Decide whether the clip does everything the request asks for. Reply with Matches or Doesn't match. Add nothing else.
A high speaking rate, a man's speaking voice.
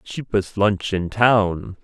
Doesn't match